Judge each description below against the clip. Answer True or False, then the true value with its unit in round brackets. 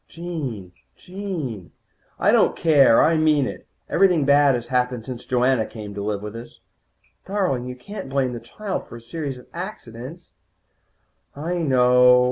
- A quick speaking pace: False (160 wpm)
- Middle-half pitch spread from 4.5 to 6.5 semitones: True (5.4 semitones)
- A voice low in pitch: True (130 Hz)